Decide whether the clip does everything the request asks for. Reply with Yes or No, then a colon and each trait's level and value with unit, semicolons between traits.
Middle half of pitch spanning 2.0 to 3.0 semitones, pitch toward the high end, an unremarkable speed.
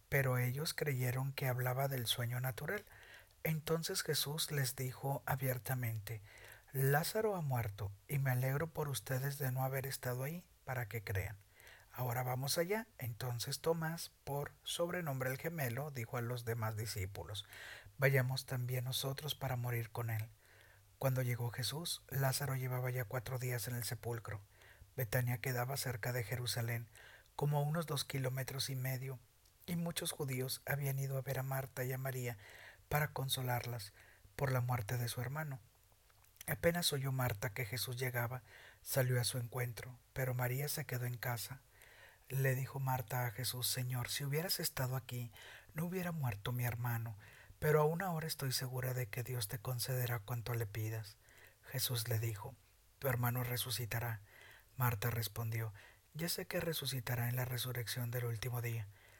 No: narrow, 2.4 semitones; low, 125 Hz; average, 155 wpm